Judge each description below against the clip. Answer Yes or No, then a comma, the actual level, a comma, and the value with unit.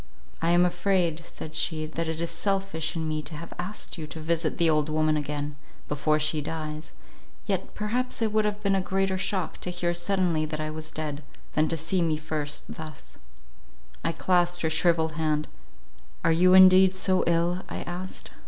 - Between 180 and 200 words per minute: Yes, average, 190 wpm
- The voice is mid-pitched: Yes, medium, 165 Hz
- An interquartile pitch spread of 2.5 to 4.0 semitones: Yes, average, 2.9 semitones